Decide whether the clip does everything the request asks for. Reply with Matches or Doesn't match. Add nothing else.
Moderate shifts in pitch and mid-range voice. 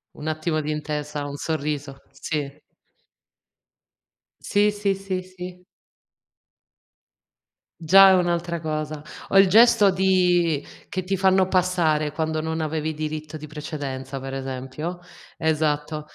Matches